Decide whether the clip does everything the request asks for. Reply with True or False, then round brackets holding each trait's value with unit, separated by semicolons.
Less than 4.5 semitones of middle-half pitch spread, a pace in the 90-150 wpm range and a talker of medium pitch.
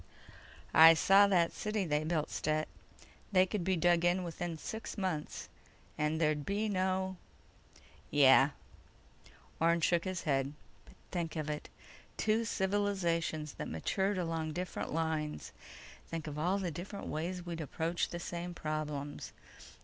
True (3.4 semitones; 140 wpm; 170 Hz)